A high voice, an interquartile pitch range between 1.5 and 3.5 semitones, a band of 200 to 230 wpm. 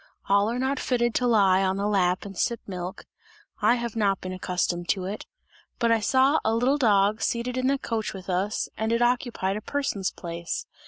No: high, 215 Hz; average, 4.0 semitones; fast, 205 wpm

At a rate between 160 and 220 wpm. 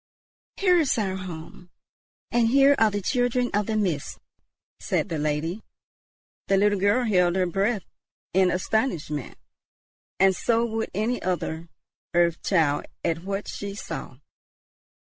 No: slow, 135 wpm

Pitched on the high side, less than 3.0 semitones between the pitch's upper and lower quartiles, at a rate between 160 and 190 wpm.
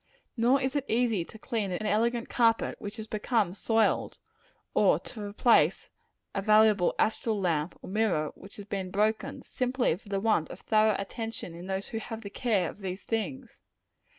Yes: high, 215 Hz; narrow, 2.6 semitones; average, 175 wpm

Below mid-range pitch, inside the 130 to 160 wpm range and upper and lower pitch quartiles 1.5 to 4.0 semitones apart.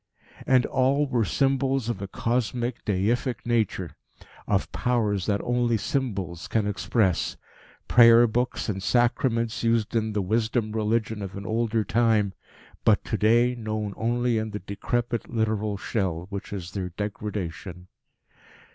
Yes: low, 110 Hz; average, 140 wpm; average, 3.0 semitones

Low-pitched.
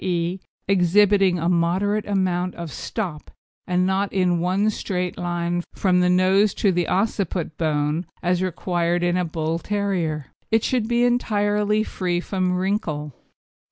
No: medium, 180 Hz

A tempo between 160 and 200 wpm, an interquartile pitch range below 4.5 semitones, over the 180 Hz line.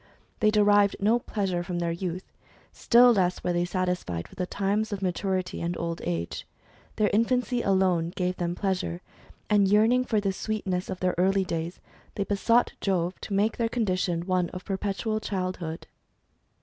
Yes: average, 165 wpm; average, 2.8 semitones; high, 190 Hz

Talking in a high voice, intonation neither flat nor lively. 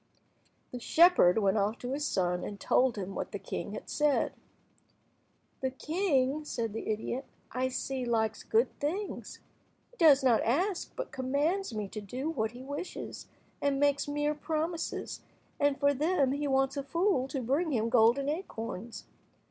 Yes: very high, 270 Hz; average, 4.5 semitones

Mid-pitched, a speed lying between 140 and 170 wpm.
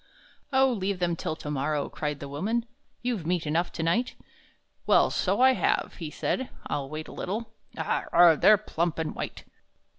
No: medium, 175 Hz; average, 180 wpm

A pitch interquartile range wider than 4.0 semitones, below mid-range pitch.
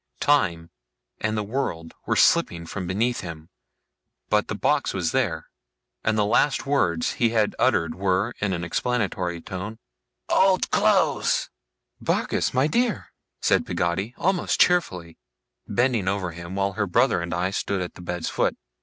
Yes: wide, 5.6 semitones; very low, 95 Hz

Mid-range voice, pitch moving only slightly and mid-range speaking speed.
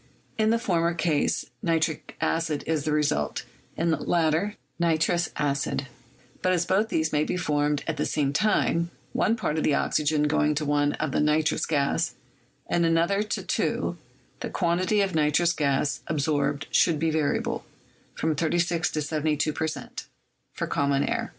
Yes: medium, 155 Hz; narrow, 2.3 semitones; average, 165 wpm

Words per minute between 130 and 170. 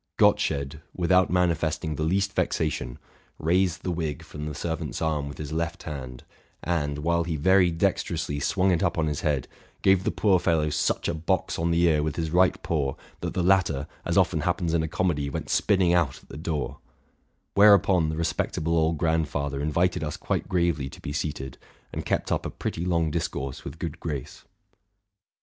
No: average, 185 wpm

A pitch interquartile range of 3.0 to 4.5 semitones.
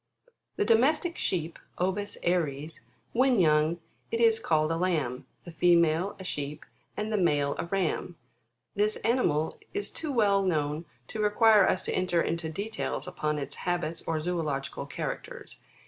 No: average, 5.0 semitones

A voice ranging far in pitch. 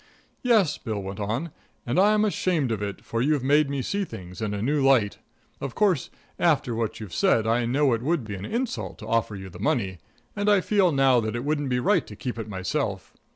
Yes: wide, 6.4 semitones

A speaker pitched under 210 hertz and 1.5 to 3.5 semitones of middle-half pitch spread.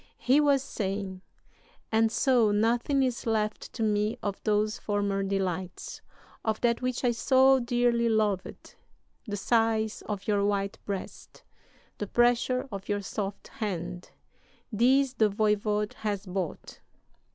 No: high, 215 Hz; average, 2.9 semitones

